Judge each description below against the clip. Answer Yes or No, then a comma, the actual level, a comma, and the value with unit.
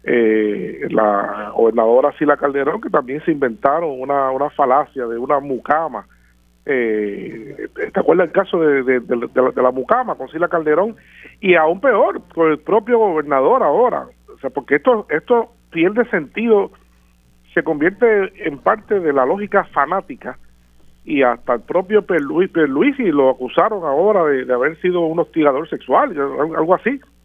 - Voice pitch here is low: No, medium, 150 Hz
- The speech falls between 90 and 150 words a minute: No, average, 165 wpm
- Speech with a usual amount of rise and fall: No, wide, 7.7 semitones